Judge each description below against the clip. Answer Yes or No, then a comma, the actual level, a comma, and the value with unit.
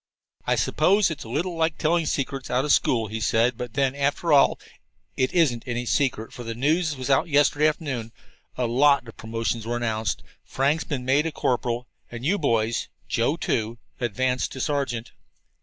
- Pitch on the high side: No, low, 130 Hz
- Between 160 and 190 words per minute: Yes, average, 180 wpm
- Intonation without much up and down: No, average, 3.9 semitones